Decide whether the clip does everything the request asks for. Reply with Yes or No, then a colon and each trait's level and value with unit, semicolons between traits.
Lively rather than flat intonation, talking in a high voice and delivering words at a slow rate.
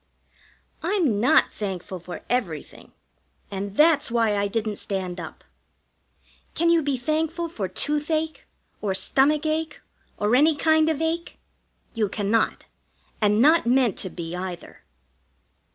Yes: wide, 7.8 semitones; high, 240 Hz; slow, 125 wpm